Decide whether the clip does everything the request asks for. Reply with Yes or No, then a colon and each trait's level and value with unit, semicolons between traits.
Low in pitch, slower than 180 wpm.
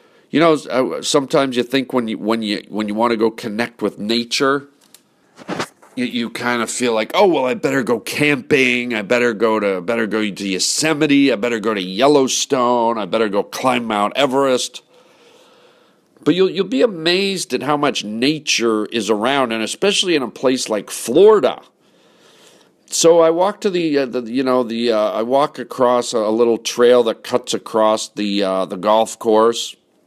No: low, 120 Hz; average, 185 wpm